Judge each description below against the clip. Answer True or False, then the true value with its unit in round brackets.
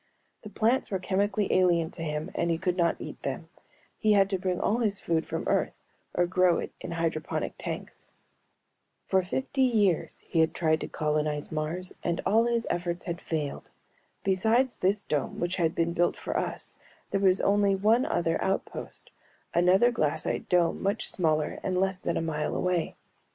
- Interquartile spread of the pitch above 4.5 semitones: False (3.3 semitones)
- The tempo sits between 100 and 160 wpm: False (175 wpm)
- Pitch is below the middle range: False (180 Hz)